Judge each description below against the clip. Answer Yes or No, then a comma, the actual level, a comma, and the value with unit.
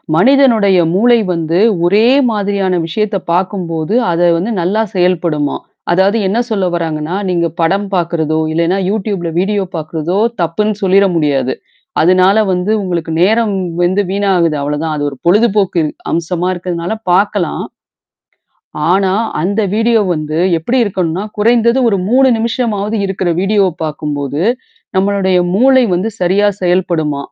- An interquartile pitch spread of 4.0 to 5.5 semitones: No, average, 3.5 semitones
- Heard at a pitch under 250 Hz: Yes, medium, 185 Hz